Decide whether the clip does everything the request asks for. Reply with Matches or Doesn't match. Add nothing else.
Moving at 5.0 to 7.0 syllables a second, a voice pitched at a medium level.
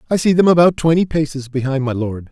Matches